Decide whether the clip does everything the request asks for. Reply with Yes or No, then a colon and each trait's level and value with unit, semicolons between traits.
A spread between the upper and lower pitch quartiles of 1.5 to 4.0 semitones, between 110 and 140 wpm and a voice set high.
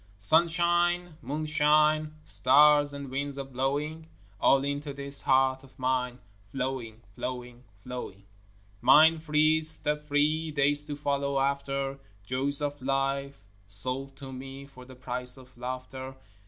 No: narrow, 2.4 semitones; slow, 135 wpm; medium, 140 Hz